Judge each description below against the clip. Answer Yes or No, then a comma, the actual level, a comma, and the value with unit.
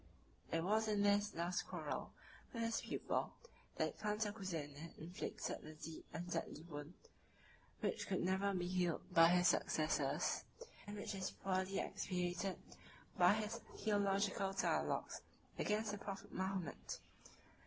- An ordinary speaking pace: No, slow, 130 wpm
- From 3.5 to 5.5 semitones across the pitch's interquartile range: No, average, 3.0 semitones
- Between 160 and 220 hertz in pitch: Yes, high, 190 Hz